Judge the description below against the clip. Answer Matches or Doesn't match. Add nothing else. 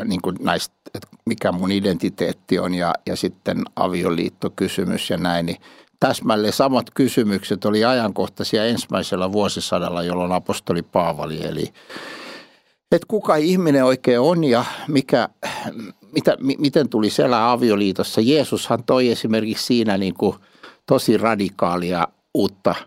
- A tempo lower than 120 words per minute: Doesn't match